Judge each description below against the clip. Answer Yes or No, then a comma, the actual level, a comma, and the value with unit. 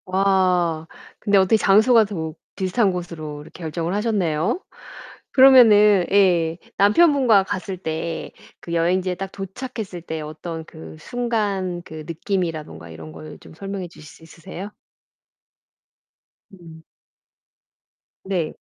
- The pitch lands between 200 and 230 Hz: No, medium, 185 Hz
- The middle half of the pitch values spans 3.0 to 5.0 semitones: Yes, average, 3.8 semitones